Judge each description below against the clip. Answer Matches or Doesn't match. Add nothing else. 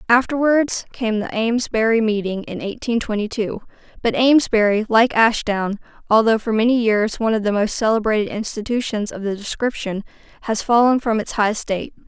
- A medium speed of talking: Matches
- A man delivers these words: Doesn't match